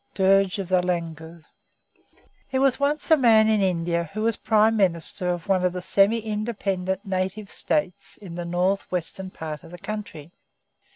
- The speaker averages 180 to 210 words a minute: No, average, 170 wpm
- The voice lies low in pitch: No, high, 190 Hz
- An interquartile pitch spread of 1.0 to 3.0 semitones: No, average, 3.4 semitones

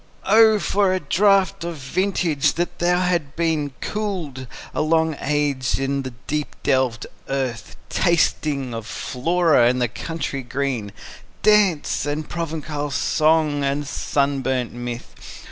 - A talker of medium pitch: Yes, medium, 145 Hz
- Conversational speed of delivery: No, slow, 125 wpm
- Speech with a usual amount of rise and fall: Yes, average, 4.3 semitones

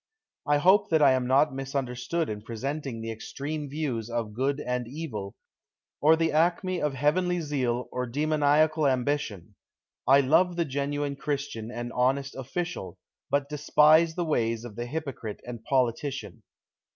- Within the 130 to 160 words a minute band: Yes, average, 150 wpm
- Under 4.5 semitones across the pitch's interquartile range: Yes, average, 4.1 semitones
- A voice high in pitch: No, medium, 140 Hz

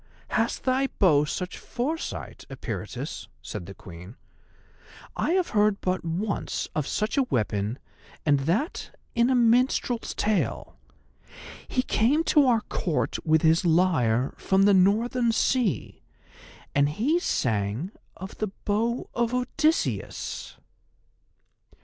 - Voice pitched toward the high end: Yes, high, 205 Hz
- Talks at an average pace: No, slow, 120 wpm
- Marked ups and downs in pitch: Yes, wide, 8.3 semitones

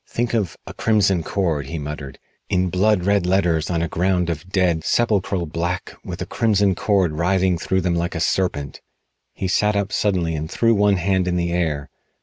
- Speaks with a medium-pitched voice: No, very low, 90 Hz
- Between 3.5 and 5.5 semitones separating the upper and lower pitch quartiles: No, average, 2.9 semitones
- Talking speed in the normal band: Yes, average, 190 wpm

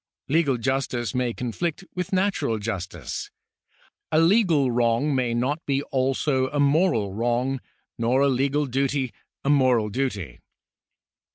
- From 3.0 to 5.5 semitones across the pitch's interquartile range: Yes, average, 3.5 semitones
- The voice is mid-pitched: No, low, 130 Hz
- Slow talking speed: Yes, slow, 125 wpm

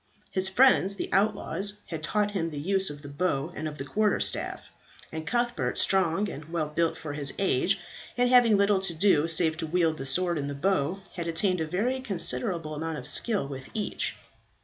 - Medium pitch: Yes, medium, 170 Hz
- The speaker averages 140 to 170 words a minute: No, average, 200 wpm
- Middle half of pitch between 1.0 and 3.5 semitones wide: No, average, 4.4 semitones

